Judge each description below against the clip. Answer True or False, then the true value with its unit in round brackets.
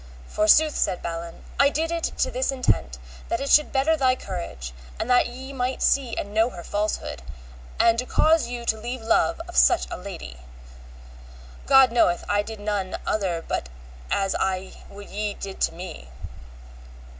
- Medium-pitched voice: False (220 Hz)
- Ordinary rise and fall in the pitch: False (5.8 semitones)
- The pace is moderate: True (170 wpm)